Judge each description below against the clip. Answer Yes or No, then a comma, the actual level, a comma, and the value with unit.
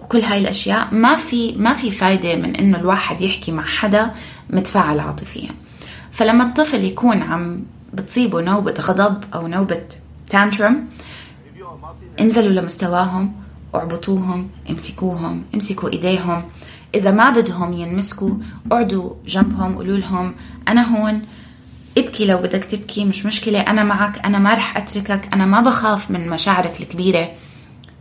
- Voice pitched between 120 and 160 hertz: No, high, 200 Hz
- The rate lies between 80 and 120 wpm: No, average, 130 wpm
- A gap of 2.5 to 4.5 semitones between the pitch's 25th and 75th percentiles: Yes, average, 3.0 semitones